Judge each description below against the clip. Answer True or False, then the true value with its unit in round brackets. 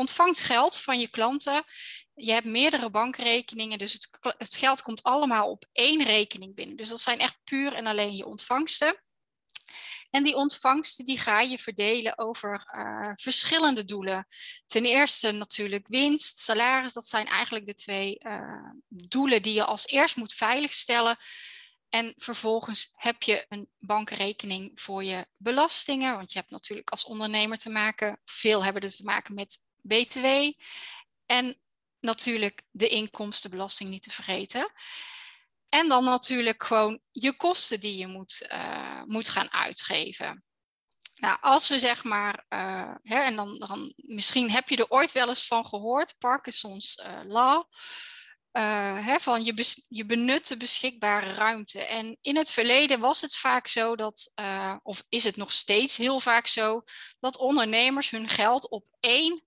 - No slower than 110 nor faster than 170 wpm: True (155 wpm)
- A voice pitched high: True (235 Hz)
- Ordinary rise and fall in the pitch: True (4.0 semitones)